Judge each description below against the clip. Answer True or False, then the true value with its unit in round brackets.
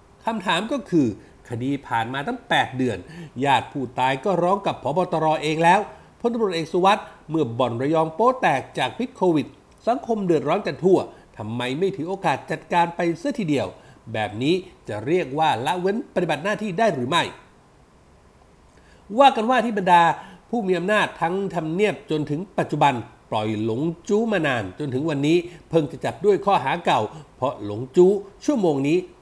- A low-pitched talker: False (170 Hz)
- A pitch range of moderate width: False (6.2 semitones)